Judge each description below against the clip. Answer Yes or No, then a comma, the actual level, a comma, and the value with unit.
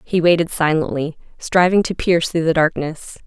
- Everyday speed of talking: Yes, average, 165 wpm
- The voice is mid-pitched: Yes, medium, 165 Hz